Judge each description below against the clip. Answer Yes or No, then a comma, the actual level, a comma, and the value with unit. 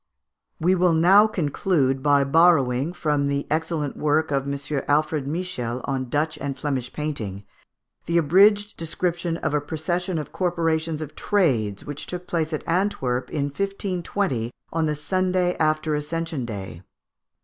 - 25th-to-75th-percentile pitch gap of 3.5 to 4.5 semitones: Yes, average, 3.8 semitones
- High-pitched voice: No, medium, 155 Hz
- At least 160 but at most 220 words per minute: No, average, 145 wpm